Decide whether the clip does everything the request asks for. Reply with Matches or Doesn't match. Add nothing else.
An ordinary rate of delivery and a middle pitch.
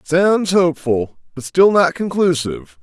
Doesn't match